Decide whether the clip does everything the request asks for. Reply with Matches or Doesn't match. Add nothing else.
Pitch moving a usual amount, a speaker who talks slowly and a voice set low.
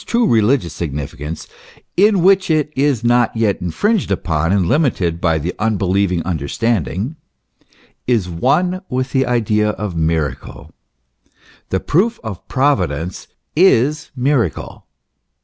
Doesn't match